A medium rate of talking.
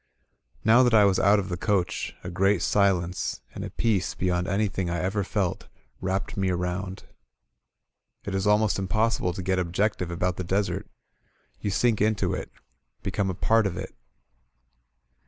Yes: average, 170 wpm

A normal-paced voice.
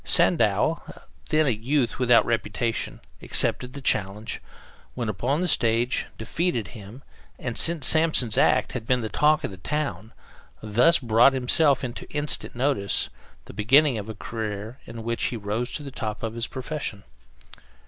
Yes: average, 160 wpm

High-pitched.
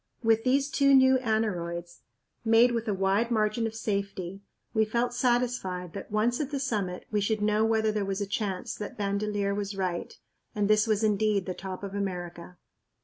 Yes: high, 210 Hz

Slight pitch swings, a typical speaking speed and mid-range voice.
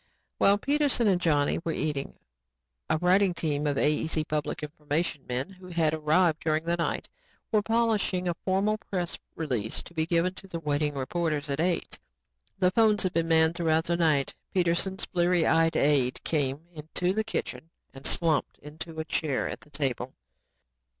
No: average, 3.4 semitones; average, 170 wpm; medium, 165 Hz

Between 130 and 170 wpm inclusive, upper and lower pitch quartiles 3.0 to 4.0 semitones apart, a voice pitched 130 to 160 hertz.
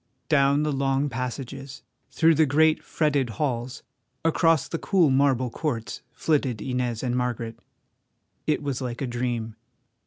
Yes: slow, 135 wpm; average, 3.3 semitones; low, 135 Hz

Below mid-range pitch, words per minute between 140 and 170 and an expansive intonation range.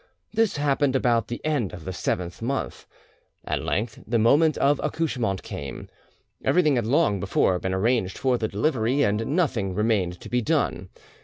Yes: low, 115 Hz; average, 165 wpm; wide, 6.5 semitones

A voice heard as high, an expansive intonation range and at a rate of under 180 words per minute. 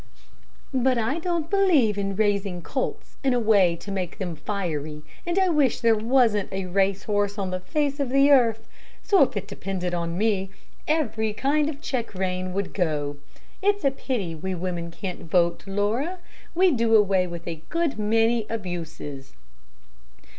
Yes: high, 205 Hz; wide, 6.4 semitones; average, 170 wpm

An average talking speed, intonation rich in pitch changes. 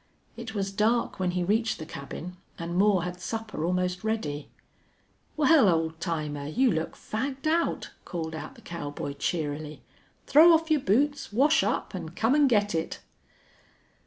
Yes: average, 160 wpm; wide, 6.8 semitones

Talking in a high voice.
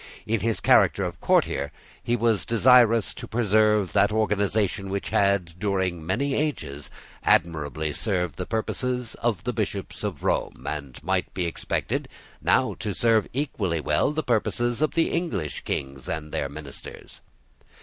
No: low, 100 Hz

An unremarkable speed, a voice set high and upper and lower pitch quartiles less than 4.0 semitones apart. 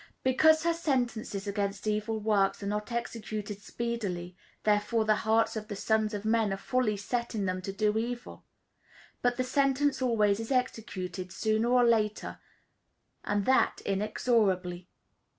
Yes: average, 150 wpm; high, 215 Hz; average, 2.8 semitones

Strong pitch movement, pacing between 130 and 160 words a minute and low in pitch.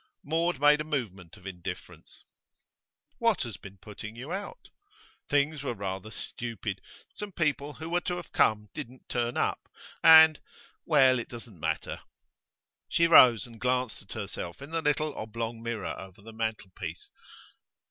Yes: wide, 6.2 semitones; average, 150 wpm; low, 120 Hz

